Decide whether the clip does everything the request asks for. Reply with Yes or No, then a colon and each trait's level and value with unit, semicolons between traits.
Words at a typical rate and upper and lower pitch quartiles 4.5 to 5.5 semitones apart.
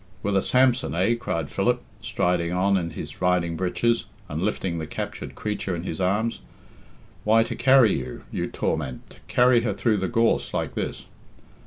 Yes: average, 175 wpm; average, 5.2 semitones